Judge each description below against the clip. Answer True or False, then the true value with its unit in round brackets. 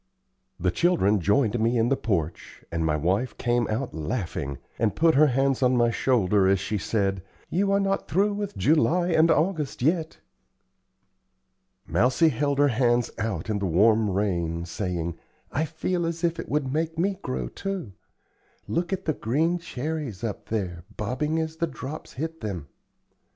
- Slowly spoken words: False (165 wpm)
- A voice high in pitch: False (125 Hz)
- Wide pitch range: True (8.2 semitones)